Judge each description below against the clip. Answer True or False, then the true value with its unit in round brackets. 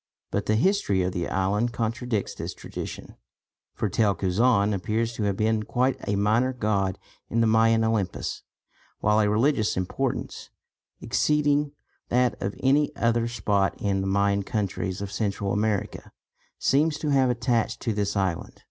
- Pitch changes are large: False (3.2 semitones)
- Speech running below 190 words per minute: True (155 wpm)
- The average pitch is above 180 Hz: False (110 Hz)